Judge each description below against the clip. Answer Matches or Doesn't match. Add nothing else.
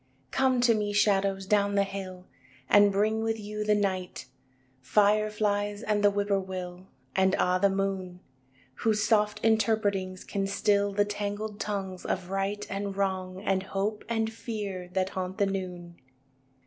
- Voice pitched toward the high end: Matches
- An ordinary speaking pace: Matches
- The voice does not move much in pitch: Matches